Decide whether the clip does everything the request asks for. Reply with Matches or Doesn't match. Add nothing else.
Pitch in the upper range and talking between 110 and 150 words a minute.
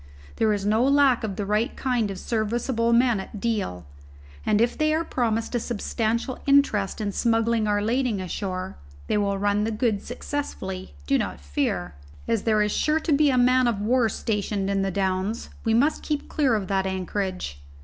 Doesn't match